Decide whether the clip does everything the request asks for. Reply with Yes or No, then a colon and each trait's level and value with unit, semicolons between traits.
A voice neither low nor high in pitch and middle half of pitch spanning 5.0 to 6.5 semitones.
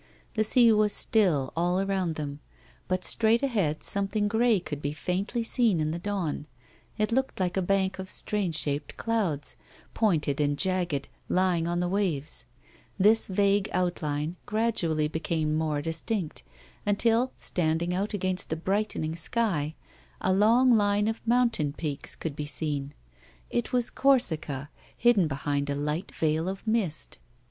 Yes: medium, 180 Hz; wide, 5.4 semitones